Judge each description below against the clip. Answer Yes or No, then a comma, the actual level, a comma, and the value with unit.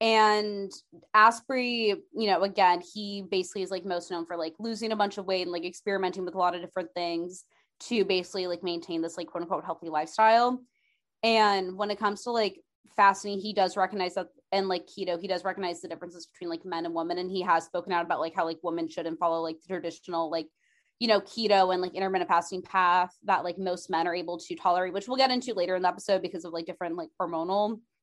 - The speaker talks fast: Yes, fast, 230 wpm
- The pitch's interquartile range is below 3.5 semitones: Yes, average, 2.7 semitones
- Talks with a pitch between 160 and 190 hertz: Yes, medium, 185 Hz